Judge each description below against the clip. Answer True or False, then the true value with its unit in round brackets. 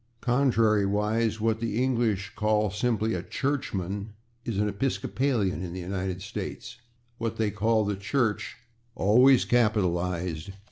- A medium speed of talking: False (125 wpm)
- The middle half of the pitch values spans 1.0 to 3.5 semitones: True (2.9 semitones)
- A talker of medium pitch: False (105 Hz)